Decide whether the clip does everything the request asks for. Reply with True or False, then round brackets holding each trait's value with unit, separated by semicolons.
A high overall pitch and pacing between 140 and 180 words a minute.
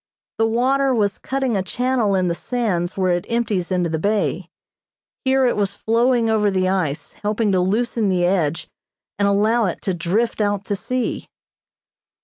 True (205 Hz; 170 wpm)